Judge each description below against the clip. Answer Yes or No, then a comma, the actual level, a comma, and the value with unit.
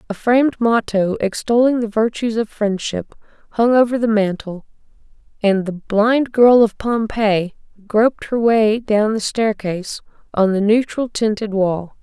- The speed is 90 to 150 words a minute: Yes, average, 145 wpm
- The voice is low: No, high, 215 Hz